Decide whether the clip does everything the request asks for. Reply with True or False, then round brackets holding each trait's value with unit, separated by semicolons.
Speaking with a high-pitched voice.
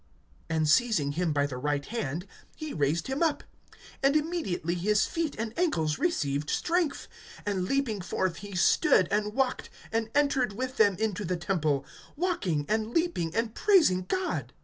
True (210 Hz)